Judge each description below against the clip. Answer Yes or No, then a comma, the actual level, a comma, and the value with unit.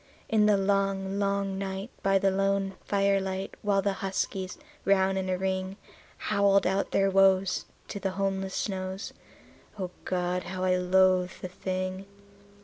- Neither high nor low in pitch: No, high, 195 Hz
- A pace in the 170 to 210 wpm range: No, average, 145 wpm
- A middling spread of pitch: No, narrow, 0.9 semitones